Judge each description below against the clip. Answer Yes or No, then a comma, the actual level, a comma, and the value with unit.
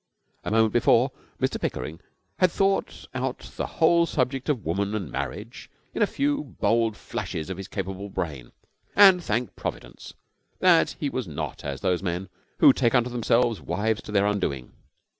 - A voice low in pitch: Yes, low, 110 Hz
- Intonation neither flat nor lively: No, wide, 5.7 semitones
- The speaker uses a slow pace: No, average, 165 wpm